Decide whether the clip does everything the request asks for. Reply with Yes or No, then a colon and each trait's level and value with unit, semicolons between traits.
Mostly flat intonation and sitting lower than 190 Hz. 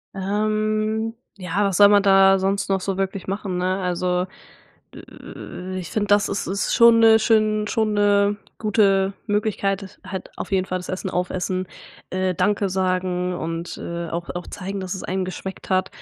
No: narrow, 1.9 semitones; high, 195 Hz